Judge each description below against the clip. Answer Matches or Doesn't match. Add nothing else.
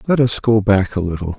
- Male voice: Matches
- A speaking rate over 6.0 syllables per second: Doesn't match